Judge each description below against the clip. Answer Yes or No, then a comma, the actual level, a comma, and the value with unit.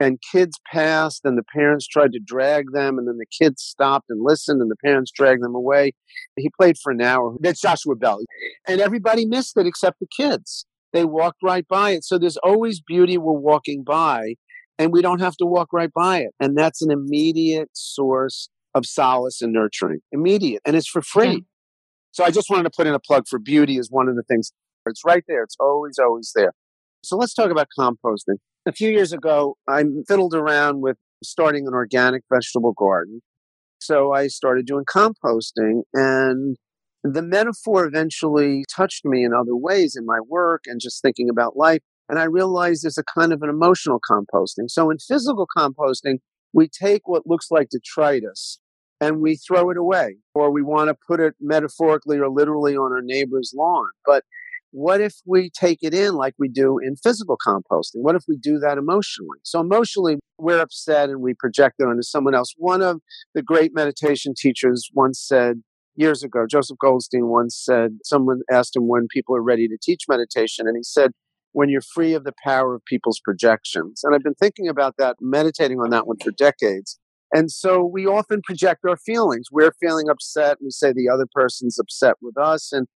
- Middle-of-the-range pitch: Yes, medium, 145 Hz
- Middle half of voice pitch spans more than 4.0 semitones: Yes, average, 4.9 semitones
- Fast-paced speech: No, average, 195 wpm